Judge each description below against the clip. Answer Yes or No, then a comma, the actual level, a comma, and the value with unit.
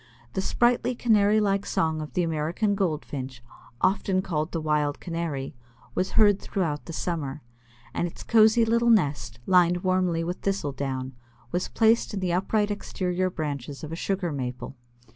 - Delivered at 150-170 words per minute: Yes, average, 160 wpm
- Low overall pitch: No, medium, 175 Hz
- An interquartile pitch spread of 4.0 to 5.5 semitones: Yes, average, 4.8 semitones